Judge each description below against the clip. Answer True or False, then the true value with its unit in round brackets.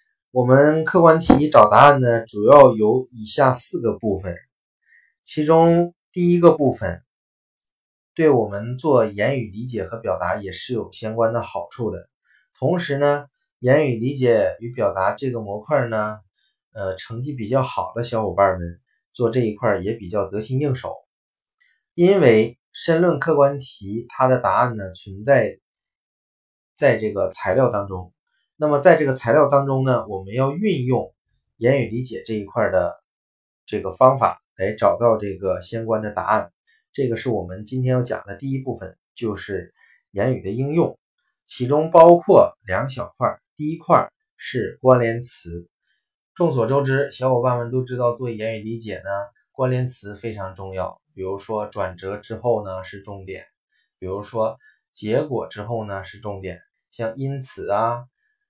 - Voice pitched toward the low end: True (120 Hz)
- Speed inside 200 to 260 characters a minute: True (230 characters per minute)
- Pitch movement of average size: True (4.8 semitones)